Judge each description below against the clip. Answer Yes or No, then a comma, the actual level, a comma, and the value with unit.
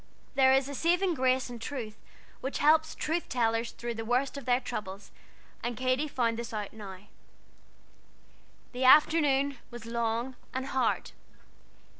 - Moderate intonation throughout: Yes, average, 3.2 semitones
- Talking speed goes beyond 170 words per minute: No, average, 145 wpm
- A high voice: Yes, very high, 255 Hz